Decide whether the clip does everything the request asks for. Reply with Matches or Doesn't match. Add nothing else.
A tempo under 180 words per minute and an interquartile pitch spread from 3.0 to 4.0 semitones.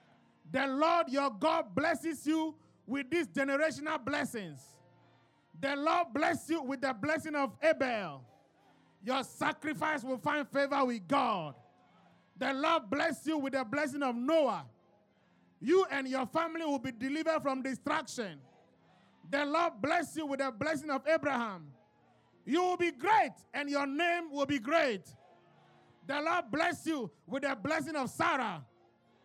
Matches